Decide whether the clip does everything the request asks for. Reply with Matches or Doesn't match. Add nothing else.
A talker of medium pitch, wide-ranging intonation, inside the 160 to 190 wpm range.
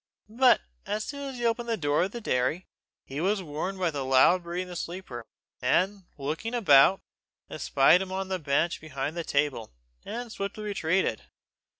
Matches